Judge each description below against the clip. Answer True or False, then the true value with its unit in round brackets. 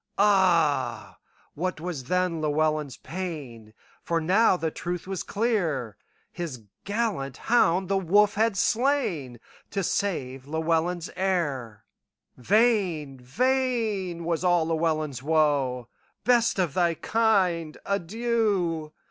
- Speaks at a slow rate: True (90 wpm)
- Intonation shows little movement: False (4.9 semitones)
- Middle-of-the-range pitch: True (170 Hz)